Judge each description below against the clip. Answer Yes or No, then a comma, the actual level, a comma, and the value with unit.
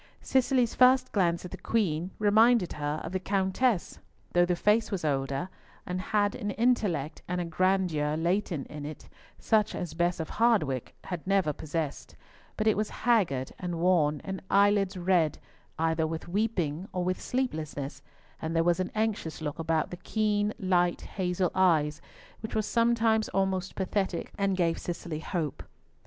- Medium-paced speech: Yes, average, 160 wpm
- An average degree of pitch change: Yes, average, 4.2 semitones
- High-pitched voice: No, medium, 180 Hz